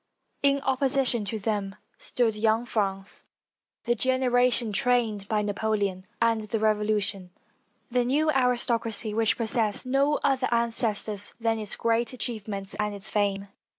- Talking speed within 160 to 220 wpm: No, average, 140 wpm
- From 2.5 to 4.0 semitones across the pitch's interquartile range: Yes, average, 3.0 semitones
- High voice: Yes, high, 225 Hz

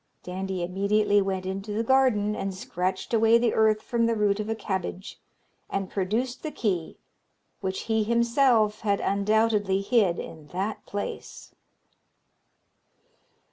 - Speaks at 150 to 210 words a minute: No, slow, 135 wpm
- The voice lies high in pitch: Yes, high, 210 Hz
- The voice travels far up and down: No, average, 2.8 semitones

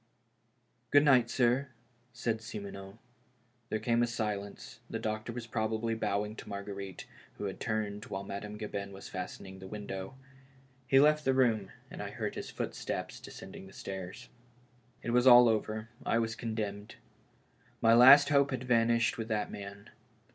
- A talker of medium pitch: No, low, 110 Hz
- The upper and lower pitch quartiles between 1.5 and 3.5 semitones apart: Yes, average, 2.8 semitones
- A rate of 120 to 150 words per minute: No, average, 160 wpm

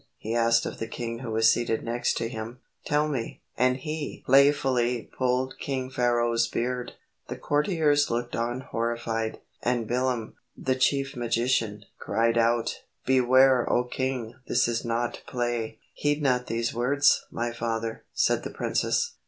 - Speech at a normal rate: Yes, average, 150 wpm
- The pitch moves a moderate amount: No, narrow, 2.1 semitones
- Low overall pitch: Yes, low, 120 Hz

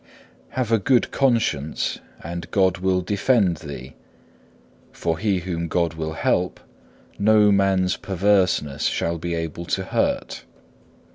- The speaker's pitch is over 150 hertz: No, very low, 90 Hz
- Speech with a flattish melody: No, average, 3.4 semitones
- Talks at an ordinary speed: No, slow, 125 wpm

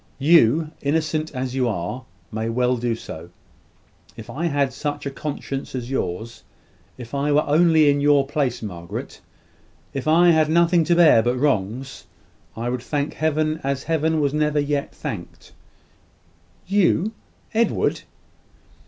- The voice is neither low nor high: Yes, medium, 145 Hz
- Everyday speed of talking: Yes, average, 145 wpm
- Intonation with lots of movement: No, average, 3.8 semitones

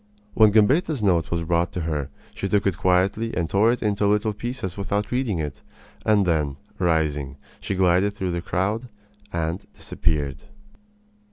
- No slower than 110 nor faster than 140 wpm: No, average, 160 wpm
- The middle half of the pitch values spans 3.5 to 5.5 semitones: Yes, average, 4.1 semitones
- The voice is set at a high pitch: No, very low, 95 Hz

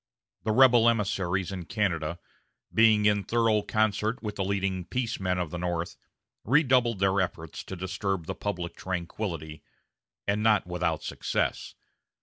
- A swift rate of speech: No, average, 140 wpm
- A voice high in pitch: No, low, 100 Hz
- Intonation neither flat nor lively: Yes, average, 3.7 semitones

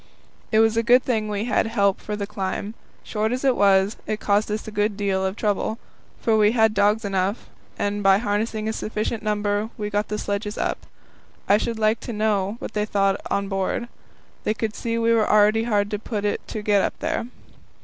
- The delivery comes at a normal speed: No, fast, 210 wpm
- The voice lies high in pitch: Yes, high, 210 Hz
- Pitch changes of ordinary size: No, narrow, 1.5 semitones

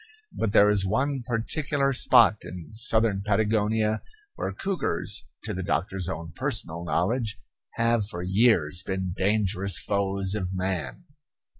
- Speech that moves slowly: Yes, slow, 130 wpm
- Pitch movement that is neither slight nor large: Yes, average, 3.4 semitones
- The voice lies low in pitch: Yes, low, 100 Hz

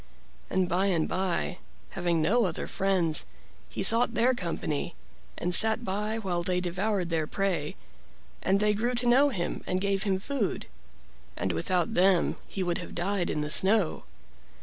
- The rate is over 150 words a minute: Yes, average, 165 wpm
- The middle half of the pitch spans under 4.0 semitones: Yes, average, 3.4 semitones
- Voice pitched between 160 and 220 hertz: Yes, high, 190 Hz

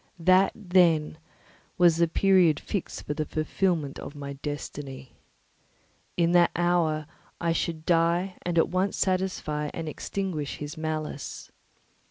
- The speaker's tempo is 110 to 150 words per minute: Yes, slow, 135 wpm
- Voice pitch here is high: No, medium, 165 Hz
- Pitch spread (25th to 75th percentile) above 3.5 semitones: No, average, 2.9 semitones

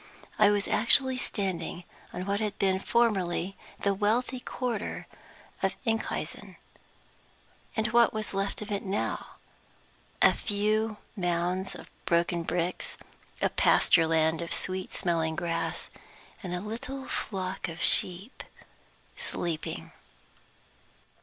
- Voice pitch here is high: Yes, high, 195 Hz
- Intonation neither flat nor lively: Yes, average, 3.7 semitones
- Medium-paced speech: No, slow, 115 wpm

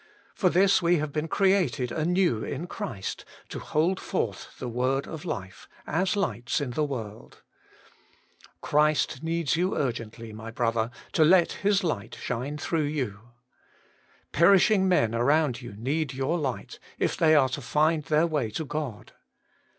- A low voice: No, medium, 150 Hz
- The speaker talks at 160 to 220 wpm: No, average, 150 wpm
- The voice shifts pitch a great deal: Yes, wide, 5.8 semitones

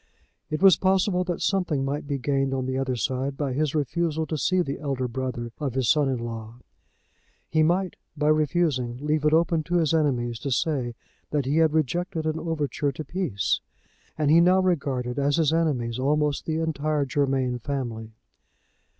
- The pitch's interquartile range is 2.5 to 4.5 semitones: Yes, average, 3.6 semitones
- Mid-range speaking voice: Yes, medium, 145 Hz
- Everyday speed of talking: Yes, average, 180 wpm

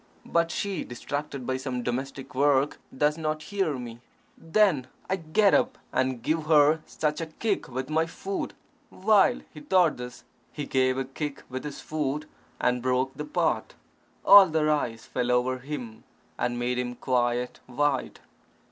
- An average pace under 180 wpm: Yes, average, 160 wpm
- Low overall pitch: No, medium, 145 Hz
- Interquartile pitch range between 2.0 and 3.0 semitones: No, average, 3.9 semitones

